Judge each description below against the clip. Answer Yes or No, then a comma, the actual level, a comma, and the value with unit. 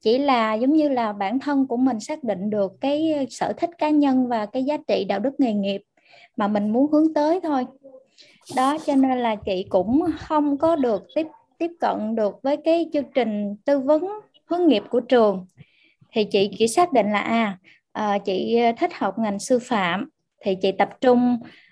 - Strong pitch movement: Yes, wide, 6.0 semitones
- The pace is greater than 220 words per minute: No, average, 195 wpm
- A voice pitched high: Yes, very high, 250 Hz